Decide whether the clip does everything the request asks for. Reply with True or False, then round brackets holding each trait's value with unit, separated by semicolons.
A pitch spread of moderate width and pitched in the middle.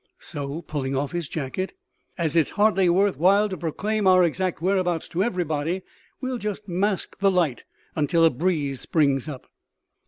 True (4.1 semitones; 175 Hz)